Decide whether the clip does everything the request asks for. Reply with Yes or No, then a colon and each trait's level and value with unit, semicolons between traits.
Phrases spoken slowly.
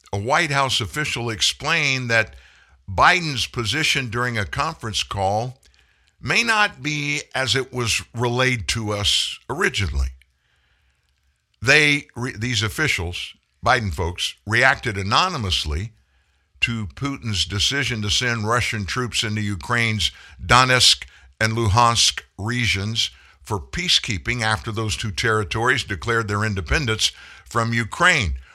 Yes: slow, 115 wpm